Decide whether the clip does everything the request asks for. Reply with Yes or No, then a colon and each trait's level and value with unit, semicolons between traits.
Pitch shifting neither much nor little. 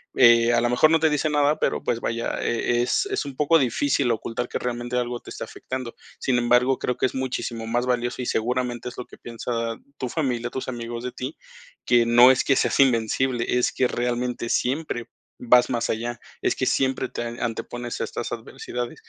No: narrow, 1.6 semitones